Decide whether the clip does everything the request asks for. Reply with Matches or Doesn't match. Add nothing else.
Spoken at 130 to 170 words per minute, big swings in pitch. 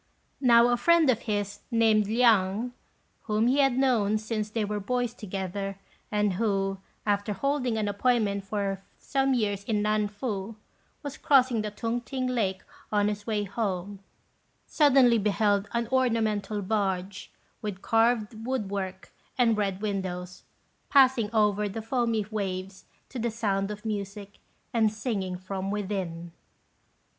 Doesn't match